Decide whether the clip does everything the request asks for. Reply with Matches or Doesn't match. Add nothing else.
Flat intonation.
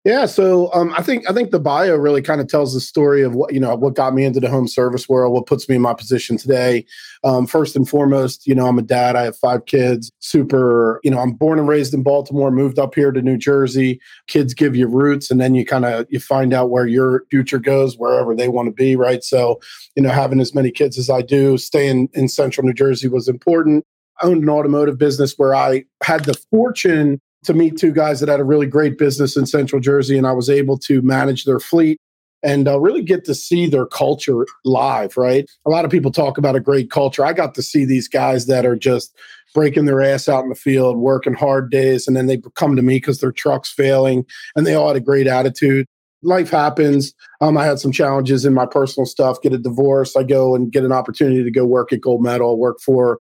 Matches